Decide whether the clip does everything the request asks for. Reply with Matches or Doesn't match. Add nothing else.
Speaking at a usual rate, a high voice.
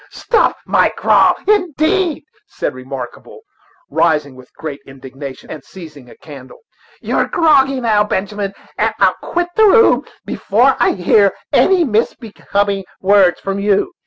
Doesn't match